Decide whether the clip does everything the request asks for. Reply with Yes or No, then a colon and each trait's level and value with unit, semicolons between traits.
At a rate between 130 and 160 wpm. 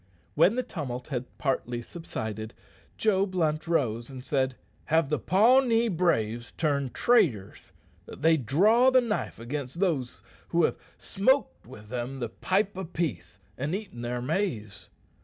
Yes: average, 145 wpm